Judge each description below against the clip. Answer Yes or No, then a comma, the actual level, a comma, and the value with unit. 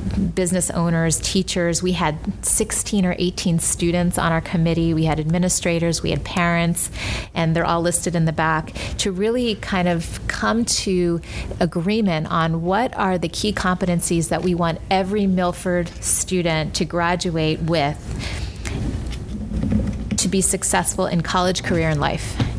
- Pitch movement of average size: No, narrow, 2.0 semitones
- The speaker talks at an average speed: Yes, average, 145 wpm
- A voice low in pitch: No, medium, 175 Hz